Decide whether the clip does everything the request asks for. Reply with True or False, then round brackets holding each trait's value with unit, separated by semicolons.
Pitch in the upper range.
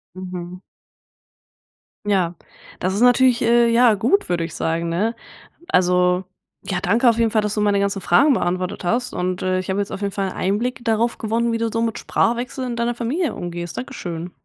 True (205 Hz)